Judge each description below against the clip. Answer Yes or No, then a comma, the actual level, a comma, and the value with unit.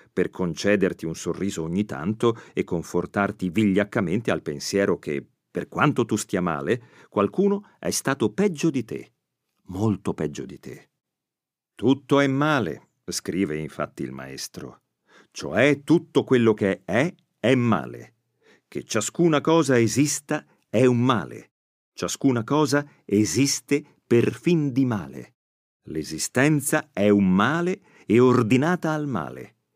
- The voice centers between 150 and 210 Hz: No, low, 125 Hz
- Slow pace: No, average, 125 wpm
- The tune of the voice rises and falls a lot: Yes, wide, 6.8 semitones